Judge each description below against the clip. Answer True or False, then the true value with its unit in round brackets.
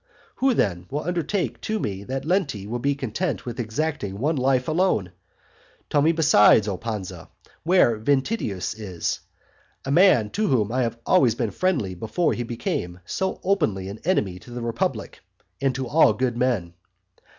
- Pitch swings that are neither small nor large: False (7.2 semitones)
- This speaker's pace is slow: False (165 wpm)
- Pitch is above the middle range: False (125 Hz)